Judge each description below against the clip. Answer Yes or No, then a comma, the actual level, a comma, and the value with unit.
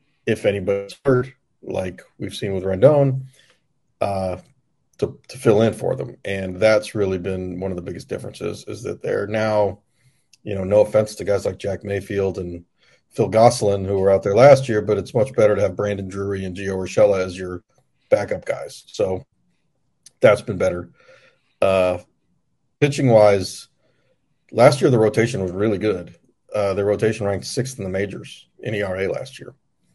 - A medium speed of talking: Yes, average, 175 wpm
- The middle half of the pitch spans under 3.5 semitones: Yes, narrow, 2.5 semitones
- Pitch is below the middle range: Yes, low, 100 Hz